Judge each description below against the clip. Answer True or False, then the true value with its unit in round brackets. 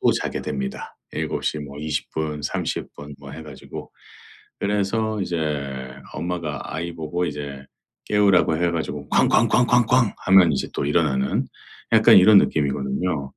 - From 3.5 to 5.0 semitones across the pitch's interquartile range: True (4.4 semitones)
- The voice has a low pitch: True (80 Hz)